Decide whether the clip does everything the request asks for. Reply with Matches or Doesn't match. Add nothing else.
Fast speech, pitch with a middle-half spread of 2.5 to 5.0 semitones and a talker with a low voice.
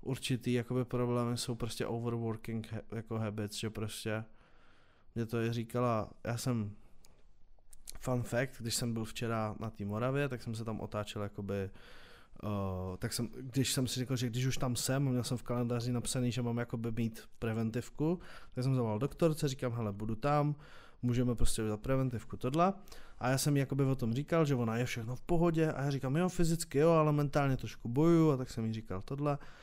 Matches